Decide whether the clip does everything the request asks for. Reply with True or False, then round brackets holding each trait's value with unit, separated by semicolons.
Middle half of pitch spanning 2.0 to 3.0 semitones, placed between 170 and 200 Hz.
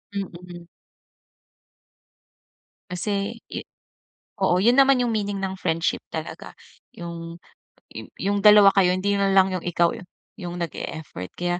True (2.6 semitones; 190 Hz)